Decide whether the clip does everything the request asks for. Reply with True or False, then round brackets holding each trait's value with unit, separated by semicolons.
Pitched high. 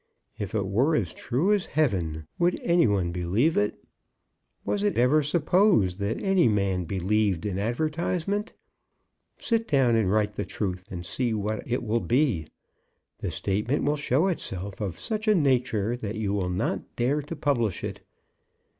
False (115 Hz)